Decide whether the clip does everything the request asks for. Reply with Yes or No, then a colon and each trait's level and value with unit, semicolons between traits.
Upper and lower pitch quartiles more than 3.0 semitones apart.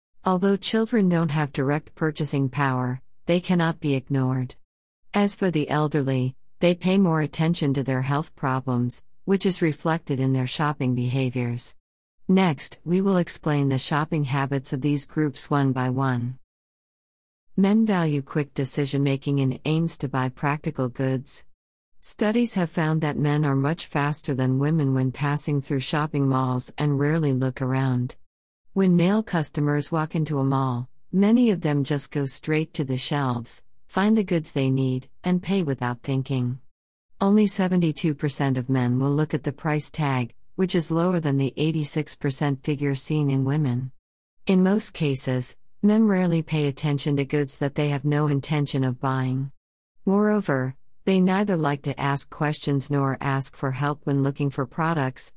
Yes: average, 3.5 semitones